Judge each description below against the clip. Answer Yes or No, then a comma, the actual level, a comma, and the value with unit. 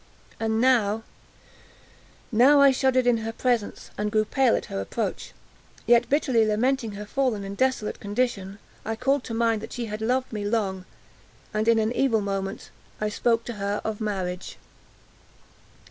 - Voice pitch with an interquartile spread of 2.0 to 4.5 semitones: Yes, average, 3.0 semitones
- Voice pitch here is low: No, high, 225 Hz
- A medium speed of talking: Yes, average, 160 wpm